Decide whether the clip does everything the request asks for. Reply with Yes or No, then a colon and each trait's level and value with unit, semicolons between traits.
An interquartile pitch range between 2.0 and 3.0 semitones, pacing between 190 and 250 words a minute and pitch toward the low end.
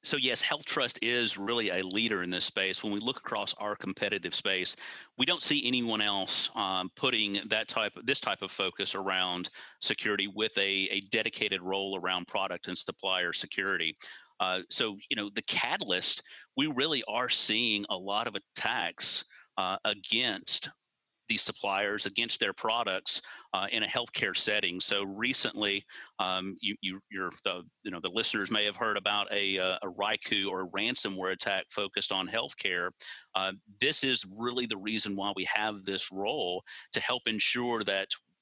No: narrow, 2.6 semitones; average, 175 wpm; low, 100 Hz